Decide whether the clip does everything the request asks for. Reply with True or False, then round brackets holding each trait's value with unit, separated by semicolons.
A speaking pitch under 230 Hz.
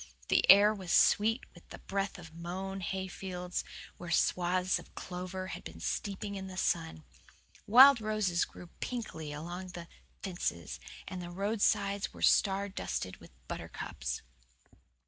True (185 Hz)